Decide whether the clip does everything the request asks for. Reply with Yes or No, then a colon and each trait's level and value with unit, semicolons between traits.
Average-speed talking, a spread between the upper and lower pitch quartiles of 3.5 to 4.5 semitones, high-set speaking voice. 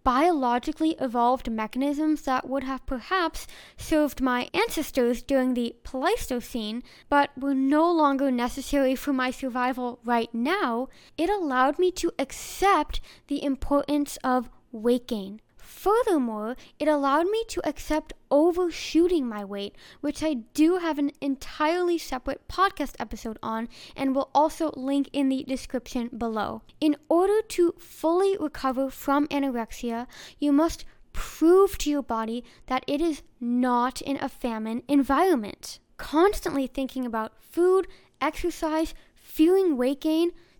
No: slow, 130 wpm; average, 4.2 semitones; very high, 280 Hz